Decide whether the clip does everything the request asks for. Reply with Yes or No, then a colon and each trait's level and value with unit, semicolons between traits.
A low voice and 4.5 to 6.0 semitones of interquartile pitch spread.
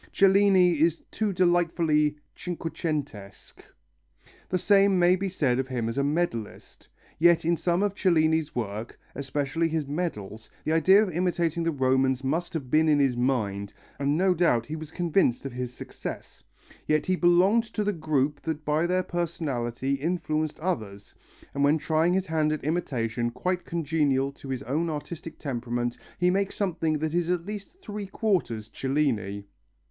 No: medium, 155 Hz; average, 4.8 semitones